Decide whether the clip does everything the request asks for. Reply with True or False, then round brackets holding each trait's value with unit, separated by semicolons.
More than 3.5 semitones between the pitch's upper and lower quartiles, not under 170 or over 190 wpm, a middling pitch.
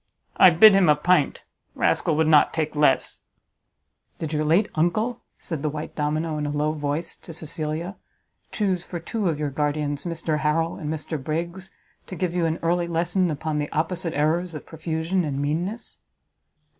False (2.5 semitones; 175 wpm; 160 Hz)